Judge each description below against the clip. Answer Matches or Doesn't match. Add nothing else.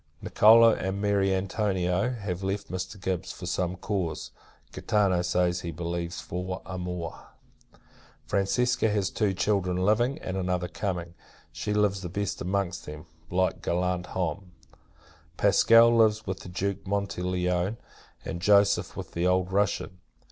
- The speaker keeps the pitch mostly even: Matches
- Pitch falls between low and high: Doesn't match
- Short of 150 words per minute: Matches